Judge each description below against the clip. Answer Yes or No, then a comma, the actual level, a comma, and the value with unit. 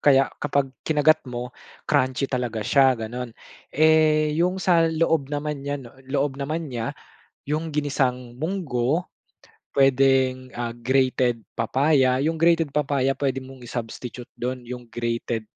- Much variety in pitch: No, average, 3.3 semitones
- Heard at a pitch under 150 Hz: Yes, low, 135 Hz